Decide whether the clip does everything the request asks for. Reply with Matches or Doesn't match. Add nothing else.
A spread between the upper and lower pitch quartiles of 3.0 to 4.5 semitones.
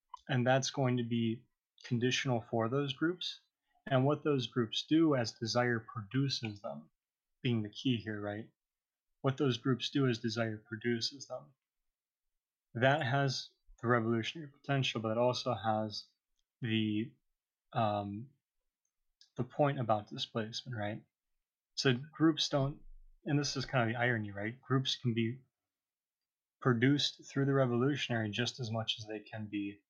Matches